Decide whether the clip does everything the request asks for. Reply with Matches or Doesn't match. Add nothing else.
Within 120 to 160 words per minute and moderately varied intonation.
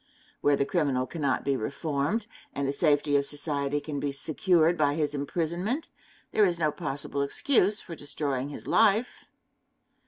Matches